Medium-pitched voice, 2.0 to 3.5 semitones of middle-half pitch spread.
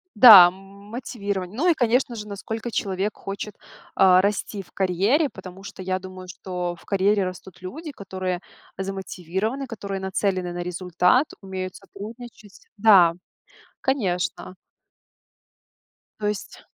No: high, 195 Hz; narrow, 2.5 semitones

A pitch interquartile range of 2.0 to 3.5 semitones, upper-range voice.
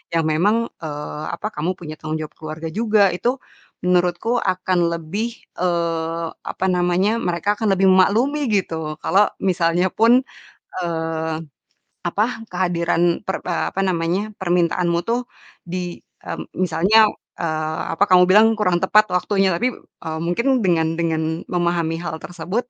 No: average, 2.7 semitones; medium, 175 Hz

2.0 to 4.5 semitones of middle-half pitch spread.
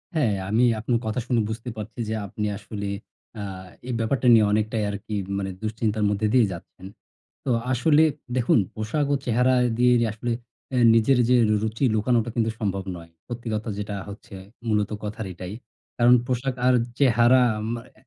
Yes: average, 2.7 semitones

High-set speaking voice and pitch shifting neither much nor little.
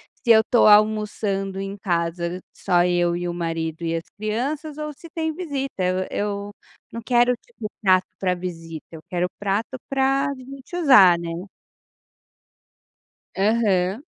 No: high, 200 Hz; wide, 6.5 semitones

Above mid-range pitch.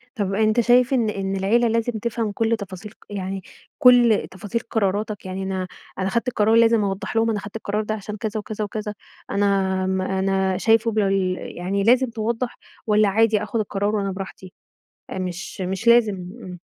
Yes: high, 210 Hz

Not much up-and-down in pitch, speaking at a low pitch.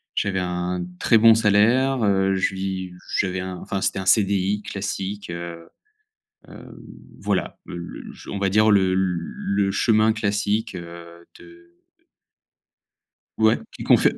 Yes: narrow, 2.3 semitones; very low, 95 Hz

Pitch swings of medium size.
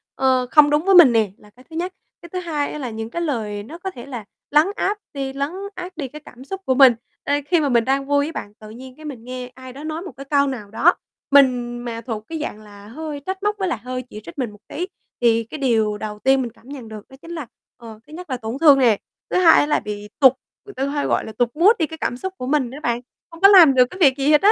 Yes: average, 4.8 semitones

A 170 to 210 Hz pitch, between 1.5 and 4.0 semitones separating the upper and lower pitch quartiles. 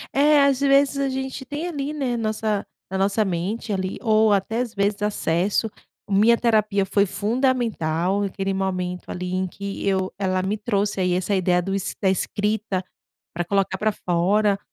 Yes: high, 205 Hz; average, 3.3 semitones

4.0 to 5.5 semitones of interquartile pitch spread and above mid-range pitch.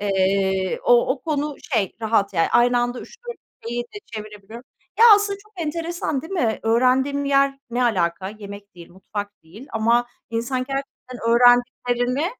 Yes: average, 4.9 semitones; high, 240 Hz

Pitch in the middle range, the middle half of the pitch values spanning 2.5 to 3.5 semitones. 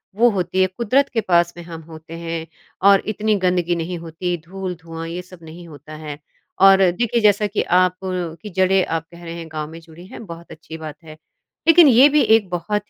Yes: medium, 175 Hz; average, 3.1 semitones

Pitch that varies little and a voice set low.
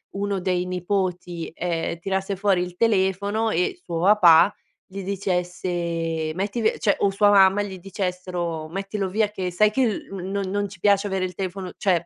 No: narrow, 2.1 semitones; high, 190 Hz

